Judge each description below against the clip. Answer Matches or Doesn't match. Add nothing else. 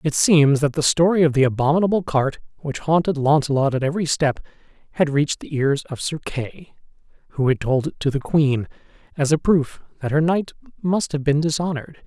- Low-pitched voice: Doesn't match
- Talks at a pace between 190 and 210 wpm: Matches